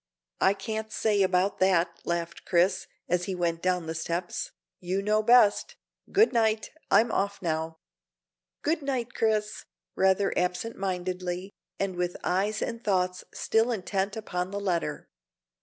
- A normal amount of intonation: Yes, average, 3.3 semitones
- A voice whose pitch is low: No, high, 190 Hz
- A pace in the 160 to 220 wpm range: No, average, 140 wpm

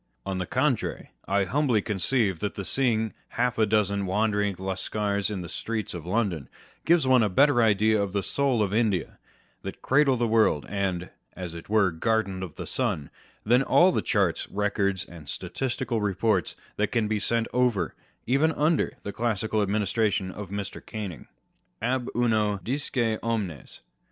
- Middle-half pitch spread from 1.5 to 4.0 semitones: Yes, average, 3.3 semitones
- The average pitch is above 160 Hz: No, low, 105 Hz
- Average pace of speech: Yes, average, 165 wpm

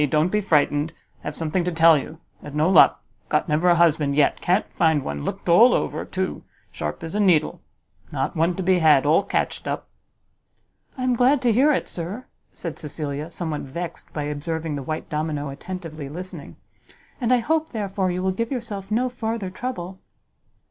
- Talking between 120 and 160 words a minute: No, average, 185 wpm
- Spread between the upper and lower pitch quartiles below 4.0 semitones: No, average, 4.9 semitones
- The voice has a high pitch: No, medium, 170 Hz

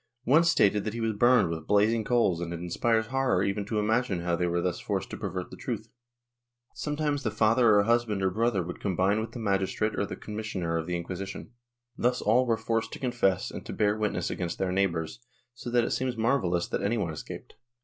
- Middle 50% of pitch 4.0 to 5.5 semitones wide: Yes, average, 4.3 semitones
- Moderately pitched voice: No, low, 105 Hz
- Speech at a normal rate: No, fast, 220 wpm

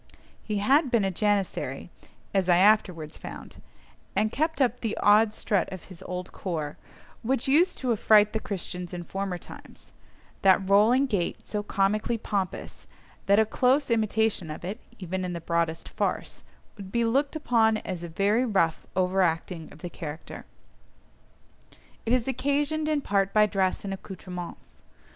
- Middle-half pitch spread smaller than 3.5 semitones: No, average, 4.1 semitones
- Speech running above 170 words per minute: No, average, 155 wpm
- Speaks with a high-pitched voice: Yes, high, 200 Hz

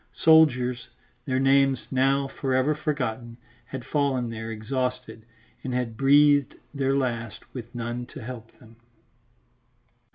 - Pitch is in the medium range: No, low, 130 Hz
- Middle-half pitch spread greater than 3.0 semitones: No, narrow, 2.6 semitones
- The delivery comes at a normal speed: No, slow, 125 wpm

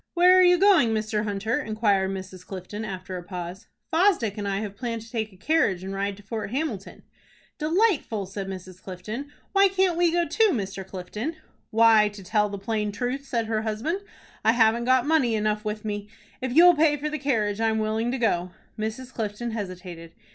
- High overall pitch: Yes, high, 220 Hz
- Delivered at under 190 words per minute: No, average, 195 wpm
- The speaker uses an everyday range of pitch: Yes, average, 4.9 semitones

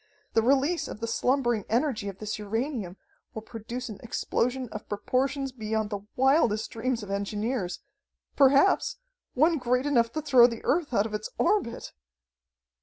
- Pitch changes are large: No, average, 3.8 semitones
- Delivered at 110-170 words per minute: Yes, average, 155 wpm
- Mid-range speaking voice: No, high, 235 Hz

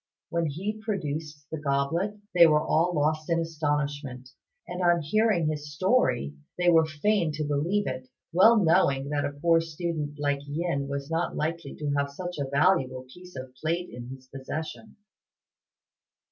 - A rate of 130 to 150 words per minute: No, average, 160 wpm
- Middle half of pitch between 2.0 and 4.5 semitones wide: Yes, average, 3.4 semitones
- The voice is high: No, medium, 155 Hz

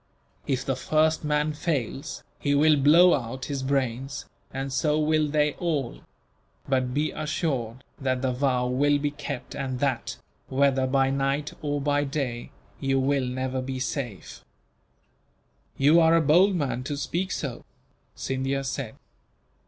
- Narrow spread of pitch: Yes, narrow, 2.3 semitones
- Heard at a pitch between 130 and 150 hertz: Yes, medium, 140 Hz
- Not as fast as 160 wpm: Yes, average, 145 wpm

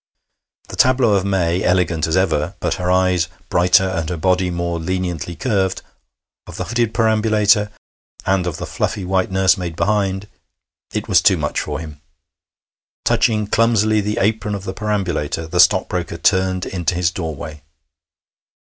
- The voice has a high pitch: No, very low, 95 Hz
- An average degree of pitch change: Yes, average, 3.0 semitones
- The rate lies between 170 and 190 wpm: No, average, 150 wpm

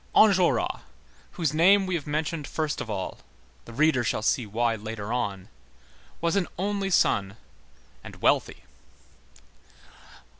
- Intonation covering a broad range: Yes, wide, 8.5 semitones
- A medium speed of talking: No, slow, 115 wpm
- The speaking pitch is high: No, medium, 140 Hz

